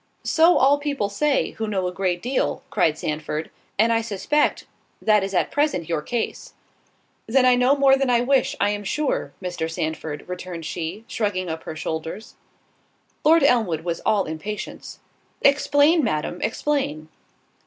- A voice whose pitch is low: No, high, 210 Hz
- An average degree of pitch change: No, wide, 8.1 semitones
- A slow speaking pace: No, average, 155 wpm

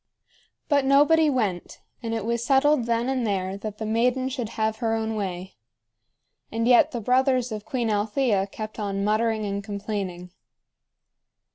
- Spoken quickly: No, average, 155 wpm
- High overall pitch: Yes, high, 225 Hz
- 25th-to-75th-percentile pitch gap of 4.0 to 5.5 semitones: No, average, 3.5 semitones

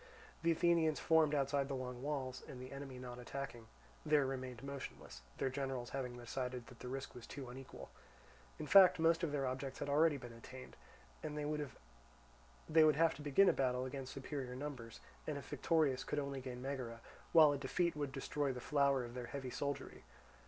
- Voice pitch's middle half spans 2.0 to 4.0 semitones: Yes, average, 2.8 semitones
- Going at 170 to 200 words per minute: Yes, average, 190 wpm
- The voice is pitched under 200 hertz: Yes, low, 135 Hz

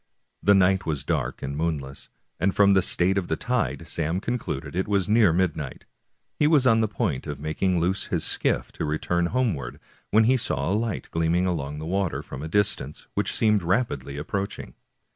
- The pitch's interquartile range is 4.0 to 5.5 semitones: Yes, average, 4.9 semitones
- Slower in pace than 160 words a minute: No, average, 195 wpm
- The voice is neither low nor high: No, very low, 90 Hz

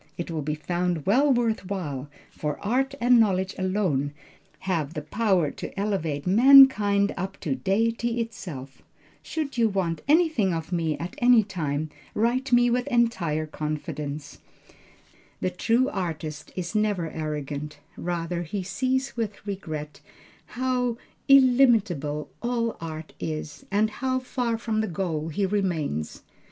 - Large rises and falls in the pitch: Yes, wide, 7.0 semitones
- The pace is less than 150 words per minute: Yes, slow, 135 wpm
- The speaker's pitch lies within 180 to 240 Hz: Yes, high, 190 Hz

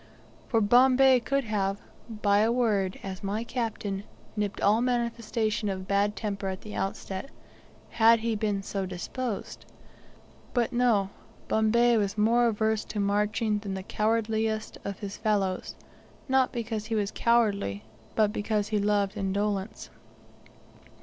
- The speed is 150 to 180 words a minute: No, slow, 135 wpm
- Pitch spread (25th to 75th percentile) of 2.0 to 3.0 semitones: Yes, narrow, 2.4 semitones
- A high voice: Yes, high, 210 Hz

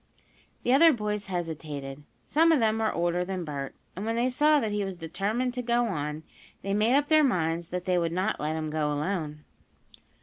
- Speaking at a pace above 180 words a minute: Yes, fast, 205 wpm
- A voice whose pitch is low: No, high, 190 Hz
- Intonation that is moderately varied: No, wide, 6.7 semitones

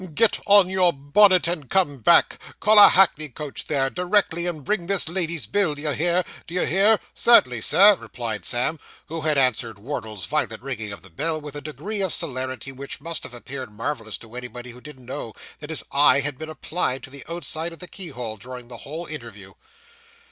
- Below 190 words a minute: No, average, 195 wpm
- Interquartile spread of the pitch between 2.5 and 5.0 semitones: No, wide, 5.6 semitones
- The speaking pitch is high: No, medium, 150 Hz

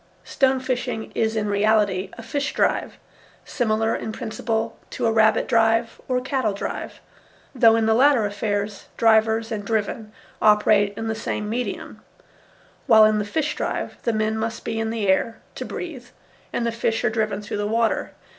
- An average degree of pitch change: No, narrow, 1.5 semitones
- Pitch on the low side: No, high, 220 Hz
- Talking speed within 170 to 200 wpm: Yes, average, 175 wpm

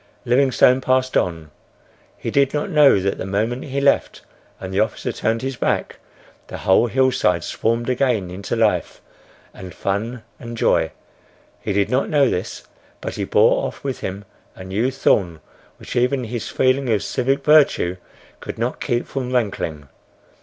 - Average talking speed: Yes, average, 160 wpm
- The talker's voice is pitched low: Yes, low, 120 Hz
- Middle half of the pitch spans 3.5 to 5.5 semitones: Yes, average, 5.0 semitones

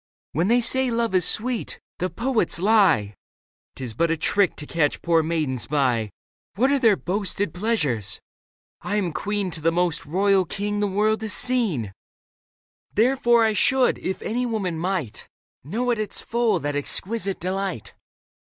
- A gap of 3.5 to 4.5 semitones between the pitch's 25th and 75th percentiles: No, wide, 5.6 semitones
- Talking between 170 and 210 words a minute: No, average, 160 wpm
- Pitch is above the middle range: Yes, high, 195 Hz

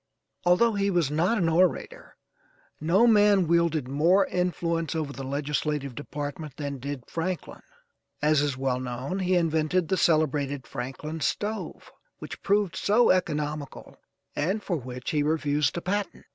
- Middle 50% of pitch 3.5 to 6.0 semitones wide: Yes, average, 4.3 semitones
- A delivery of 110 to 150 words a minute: Yes, average, 145 wpm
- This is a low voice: No, medium, 160 Hz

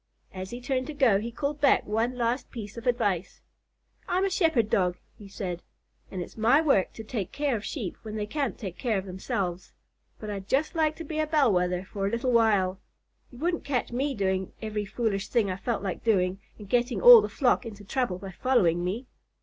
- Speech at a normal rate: No, fast, 215 wpm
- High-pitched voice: Yes, high, 225 Hz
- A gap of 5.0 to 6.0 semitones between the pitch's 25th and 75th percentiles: Yes, average, 5.3 semitones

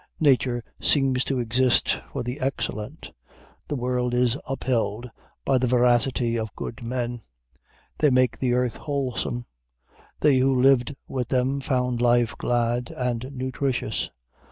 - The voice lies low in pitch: Yes, low, 125 Hz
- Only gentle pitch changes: Yes, narrow, 1.5 semitones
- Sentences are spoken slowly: Yes, slow, 130 wpm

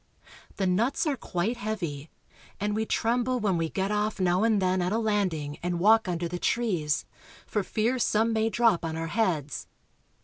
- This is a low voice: No, high, 205 Hz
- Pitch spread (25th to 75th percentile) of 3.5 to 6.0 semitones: Yes, average, 4.3 semitones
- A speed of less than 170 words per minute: No, average, 190 wpm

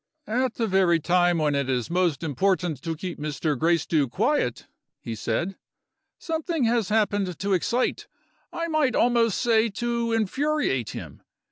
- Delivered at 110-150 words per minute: Yes, average, 145 wpm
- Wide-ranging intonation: Yes, wide, 6.7 semitones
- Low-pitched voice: No, high, 190 Hz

